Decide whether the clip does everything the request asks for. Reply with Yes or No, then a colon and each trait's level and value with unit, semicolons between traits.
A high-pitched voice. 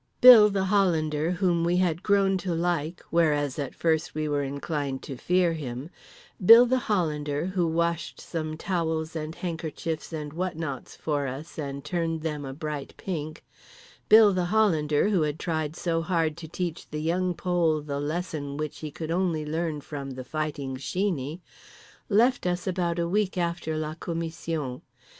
No: medium, 160 Hz